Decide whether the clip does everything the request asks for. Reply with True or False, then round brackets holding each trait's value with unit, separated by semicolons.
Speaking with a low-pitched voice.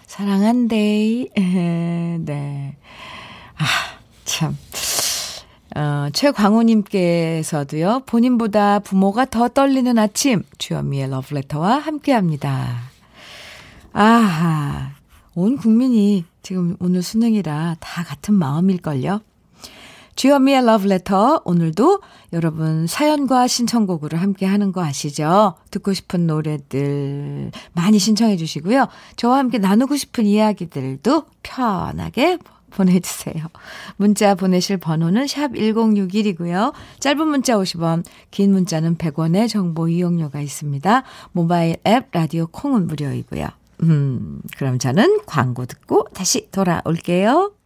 False (190 Hz)